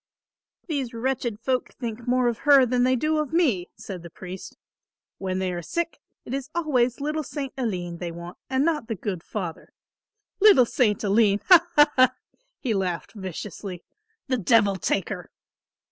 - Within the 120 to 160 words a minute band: No, average, 170 wpm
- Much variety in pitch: Yes, wide, 6.2 semitones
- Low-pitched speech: No, high, 235 Hz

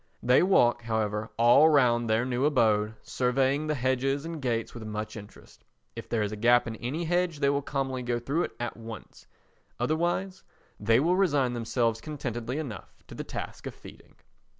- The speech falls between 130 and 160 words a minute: No, average, 180 wpm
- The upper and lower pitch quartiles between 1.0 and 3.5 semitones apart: No, average, 4.0 semitones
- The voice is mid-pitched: No, low, 125 Hz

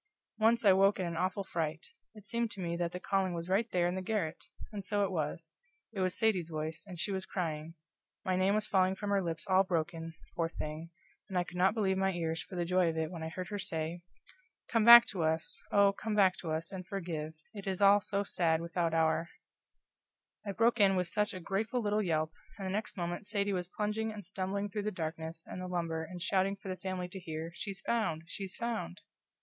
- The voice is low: No, medium, 185 Hz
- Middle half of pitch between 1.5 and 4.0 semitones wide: Yes, average, 3.3 semitones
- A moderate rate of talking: No, fast, 230 wpm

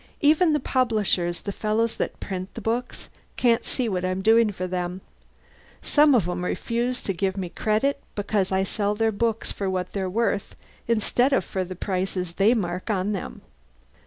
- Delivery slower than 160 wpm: No, average, 170 wpm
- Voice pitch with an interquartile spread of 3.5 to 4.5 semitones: Yes, average, 3.9 semitones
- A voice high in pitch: Yes, high, 205 Hz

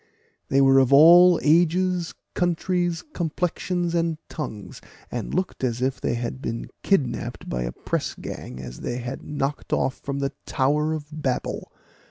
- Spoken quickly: No, average, 150 wpm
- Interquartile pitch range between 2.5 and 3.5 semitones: No, average, 5.1 semitones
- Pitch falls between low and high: Yes, medium, 145 Hz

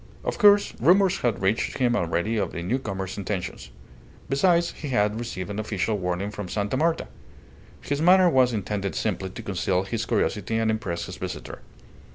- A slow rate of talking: No, average, 170 wpm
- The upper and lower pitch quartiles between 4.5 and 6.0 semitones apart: Yes, wide, 5.6 semitones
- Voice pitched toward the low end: Yes, low, 110 Hz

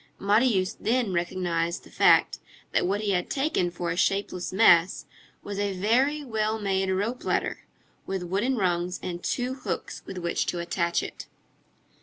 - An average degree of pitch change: Yes, average, 3.8 semitones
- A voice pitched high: Yes, high, 195 Hz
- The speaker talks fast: No, average, 160 wpm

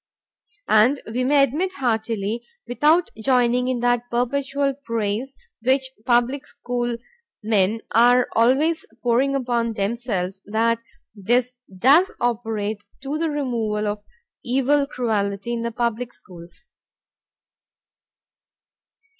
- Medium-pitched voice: No, high, 240 Hz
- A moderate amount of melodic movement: Yes, average, 3.3 semitones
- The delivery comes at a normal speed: No, slow, 110 wpm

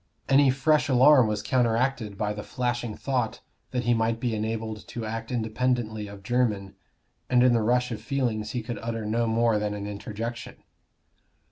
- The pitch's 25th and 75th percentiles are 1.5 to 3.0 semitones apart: Yes, narrow, 2.6 semitones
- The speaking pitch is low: Yes, low, 115 Hz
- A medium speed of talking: Yes, average, 170 wpm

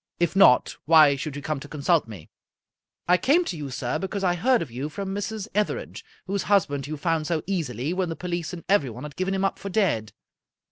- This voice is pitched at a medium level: Yes, medium, 170 Hz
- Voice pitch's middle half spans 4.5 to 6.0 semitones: Yes, average, 5.2 semitones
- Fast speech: Yes, fast, 225 wpm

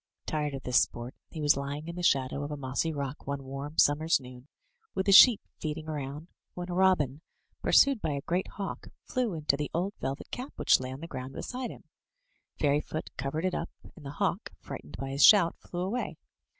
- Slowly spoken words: No, fast, 205 wpm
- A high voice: No, medium, 150 Hz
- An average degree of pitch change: Yes, average, 4.3 semitones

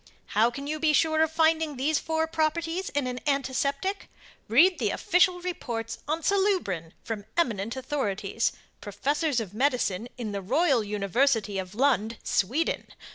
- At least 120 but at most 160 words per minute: Yes, average, 145 wpm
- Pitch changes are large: Yes, wide, 6.5 semitones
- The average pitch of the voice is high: Yes, very high, 275 Hz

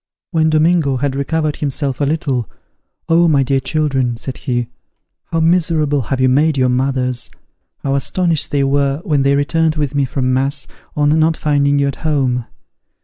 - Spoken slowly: No, average, 170 wpm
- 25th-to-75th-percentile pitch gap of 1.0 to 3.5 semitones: Yes, average, 2.7 semitones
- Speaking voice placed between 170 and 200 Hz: No, medium, 140 Hz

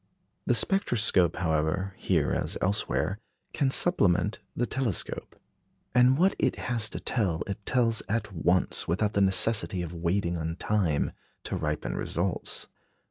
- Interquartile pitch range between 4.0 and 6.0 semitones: Yes, average, 5.0 semitones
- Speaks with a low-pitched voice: Yes, low, 100 Hz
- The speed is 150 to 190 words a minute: No, slow, 135 wpm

